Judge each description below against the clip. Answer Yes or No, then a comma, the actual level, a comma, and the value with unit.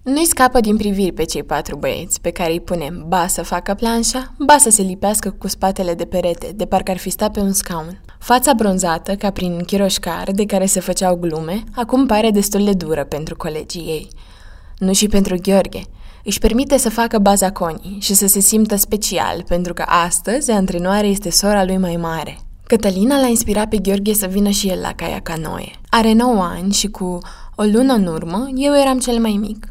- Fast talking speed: Yes, fast, 205 wpm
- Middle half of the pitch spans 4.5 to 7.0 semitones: No, average, 3.6 semitones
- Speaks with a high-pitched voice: Yes, high, 195 Hz